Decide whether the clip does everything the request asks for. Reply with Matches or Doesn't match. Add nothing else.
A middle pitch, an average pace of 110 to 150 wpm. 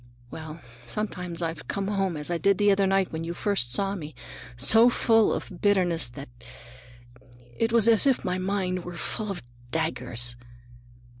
Doesn't match